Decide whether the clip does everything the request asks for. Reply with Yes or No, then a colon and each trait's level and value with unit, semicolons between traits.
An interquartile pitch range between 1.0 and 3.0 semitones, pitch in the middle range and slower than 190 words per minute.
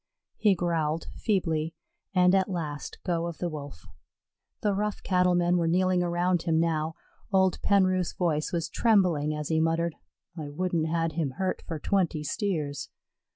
Yes: narrow, 2.6 semitones; medium, 170 Hz; average, 155 wpm